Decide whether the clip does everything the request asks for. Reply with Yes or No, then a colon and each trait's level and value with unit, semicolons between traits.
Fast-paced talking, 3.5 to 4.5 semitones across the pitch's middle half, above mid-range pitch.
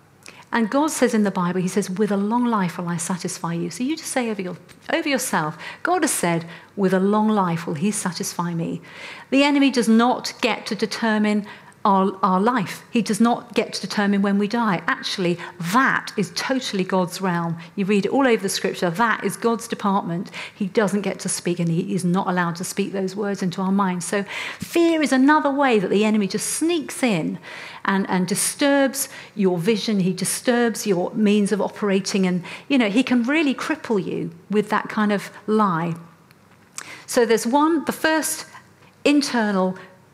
No: average, 195 wpm; average, 4.2 semitones; high, 205 Hz